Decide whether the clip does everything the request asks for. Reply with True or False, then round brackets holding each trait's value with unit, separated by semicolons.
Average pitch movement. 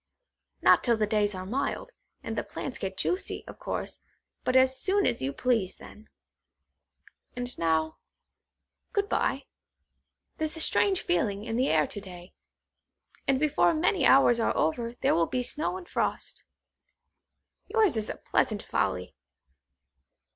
False (7.8 semitones)